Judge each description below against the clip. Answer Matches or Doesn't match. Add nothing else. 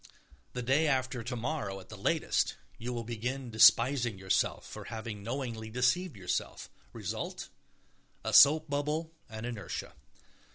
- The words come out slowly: Matches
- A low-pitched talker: Matches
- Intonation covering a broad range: Doesn't match